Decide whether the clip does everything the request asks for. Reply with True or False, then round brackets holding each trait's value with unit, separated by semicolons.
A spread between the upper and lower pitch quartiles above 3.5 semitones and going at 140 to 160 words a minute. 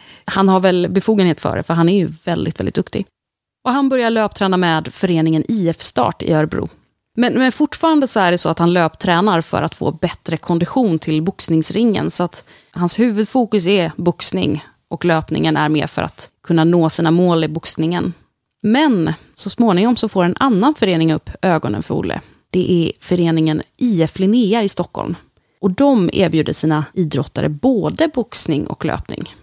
False (5.1 semitones; 175 wpm)